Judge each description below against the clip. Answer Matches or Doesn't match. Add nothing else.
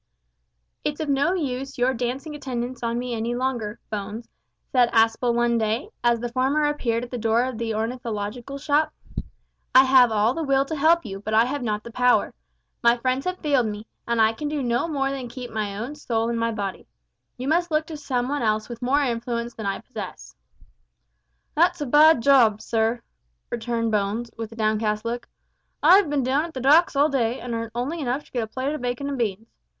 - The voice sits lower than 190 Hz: Doesn't match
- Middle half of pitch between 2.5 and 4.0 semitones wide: Matches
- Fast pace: Matches